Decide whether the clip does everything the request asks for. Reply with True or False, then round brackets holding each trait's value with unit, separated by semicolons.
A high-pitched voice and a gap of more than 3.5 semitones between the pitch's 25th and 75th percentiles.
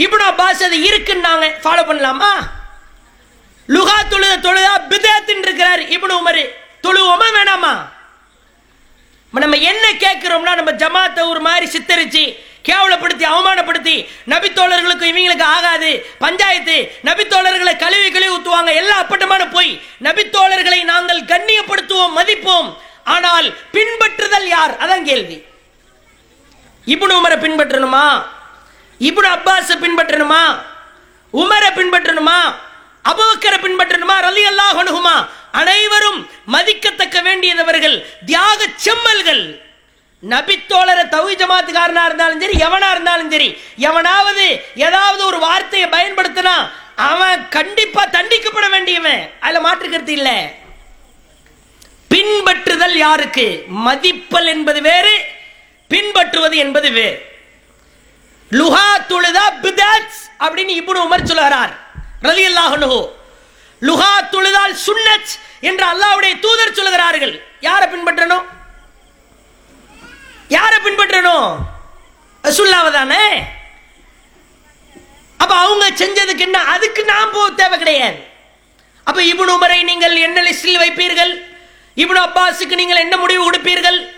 False (360 Hz; 2.6 semitones)